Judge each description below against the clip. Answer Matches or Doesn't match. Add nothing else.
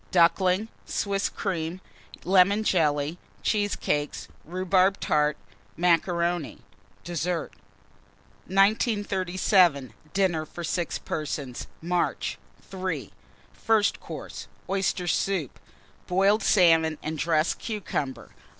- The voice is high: Doesn't match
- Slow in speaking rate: Matches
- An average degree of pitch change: Matches